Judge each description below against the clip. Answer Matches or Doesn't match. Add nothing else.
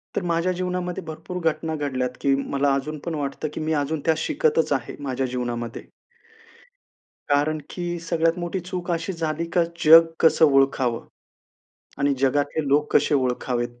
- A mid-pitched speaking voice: Matches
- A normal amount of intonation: Matches